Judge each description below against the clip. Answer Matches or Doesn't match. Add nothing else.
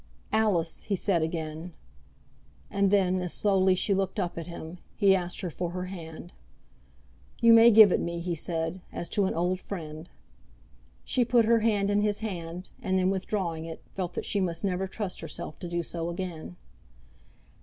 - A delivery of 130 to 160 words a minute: Doesn't match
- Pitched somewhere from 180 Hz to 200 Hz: Matches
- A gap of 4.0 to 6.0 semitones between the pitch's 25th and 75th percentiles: Doesn't match